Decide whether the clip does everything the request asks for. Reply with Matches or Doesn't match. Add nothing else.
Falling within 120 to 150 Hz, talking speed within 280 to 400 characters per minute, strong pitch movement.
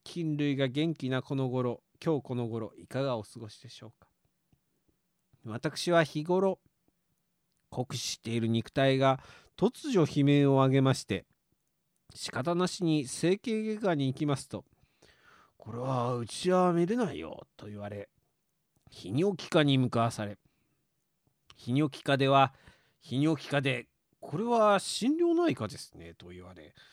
Doesn't match